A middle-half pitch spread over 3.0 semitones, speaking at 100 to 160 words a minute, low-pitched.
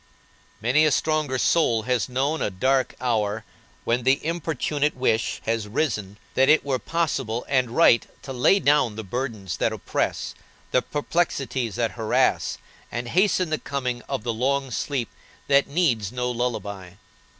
Yes: average, 3.8 semitones; average, 150 wpm; low, 125 Hz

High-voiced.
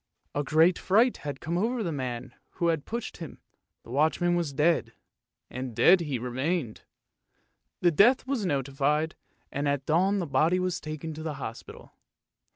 No: medium, 155 Hz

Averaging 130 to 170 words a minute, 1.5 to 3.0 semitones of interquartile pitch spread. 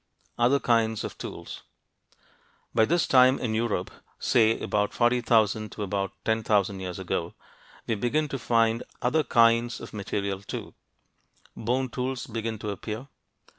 Yes: average, 140 wpm; narrow, 2.5 semitones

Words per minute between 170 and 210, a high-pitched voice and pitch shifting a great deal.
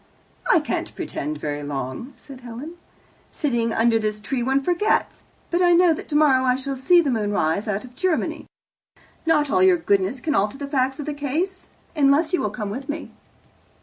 Yes: average, 190 wpm; very high, 265 Hz; wide, 6.1 semitones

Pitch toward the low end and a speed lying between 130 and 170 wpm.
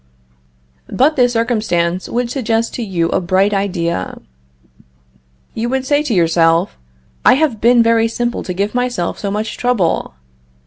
No: high, 225 Hz; average, 145 wpm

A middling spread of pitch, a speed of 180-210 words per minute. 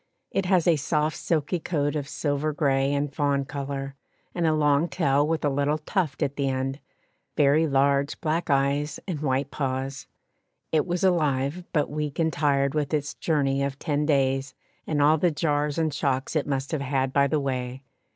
No: narrow, 2.0 semitones; average, 185 wpm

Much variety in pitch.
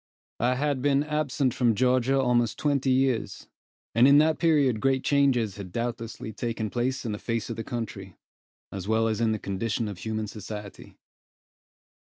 No: average, 3.5 semitones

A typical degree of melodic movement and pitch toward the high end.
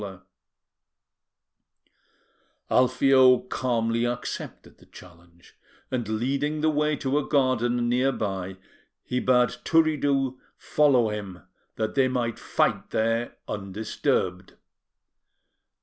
No: average, 3.6 semitones; low, 125 Hz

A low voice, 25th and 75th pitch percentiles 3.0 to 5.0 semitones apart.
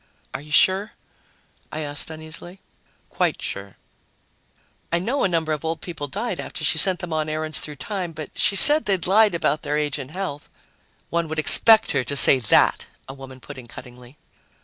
No: medium, 155 Hz; average, 4.4 semitones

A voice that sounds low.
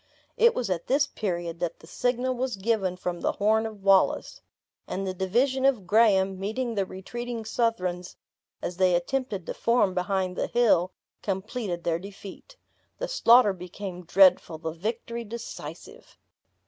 No: high, 195 Hz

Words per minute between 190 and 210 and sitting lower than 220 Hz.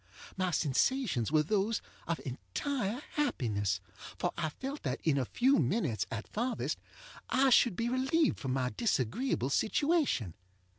No: average, 140 wpm; medium, 185 Hz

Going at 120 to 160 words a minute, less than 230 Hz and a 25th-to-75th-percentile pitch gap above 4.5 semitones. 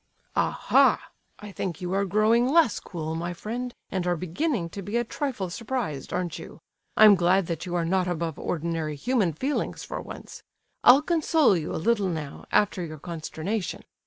No: average, 175 wpm; medium, 185 Hz; wide, 5.4 semitones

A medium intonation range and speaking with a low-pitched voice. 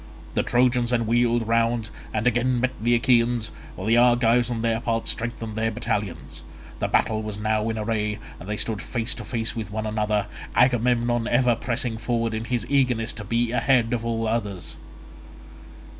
No: narrow, 1.7 semitones; low, 115 Hz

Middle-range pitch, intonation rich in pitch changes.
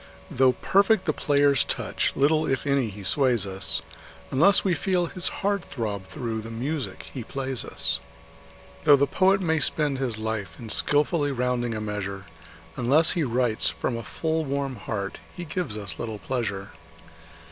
No: low, 130 Hz; wide, 5.7 semitones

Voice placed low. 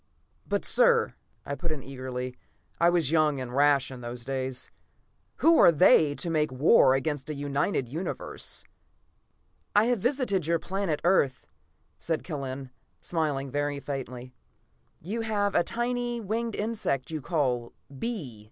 No: medium, 150 Hz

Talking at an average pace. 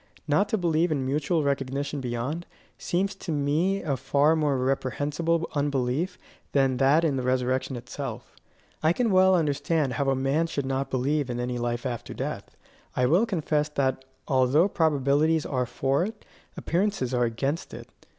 Yes: average, 160 wpm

